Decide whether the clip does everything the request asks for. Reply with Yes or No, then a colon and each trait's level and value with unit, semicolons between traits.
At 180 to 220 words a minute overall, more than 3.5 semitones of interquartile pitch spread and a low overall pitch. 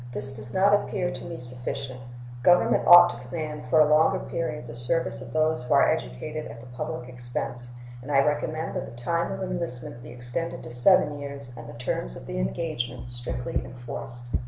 Yes: average, 195 wpm; average, 4.5 semitones; low, 125 Hz